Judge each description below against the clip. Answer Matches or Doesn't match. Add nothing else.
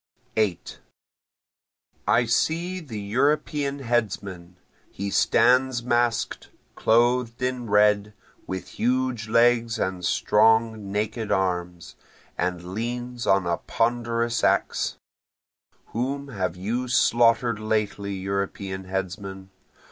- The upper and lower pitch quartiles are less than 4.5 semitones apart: Matches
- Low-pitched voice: Matches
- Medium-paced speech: Doesn't match